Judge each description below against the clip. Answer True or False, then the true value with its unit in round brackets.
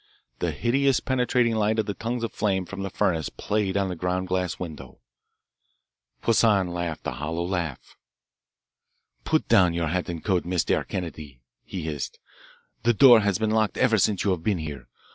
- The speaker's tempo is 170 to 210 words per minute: True (175 wpm)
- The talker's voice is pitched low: True (95 Hz)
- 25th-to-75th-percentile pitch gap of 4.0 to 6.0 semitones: True (4.3 semitones)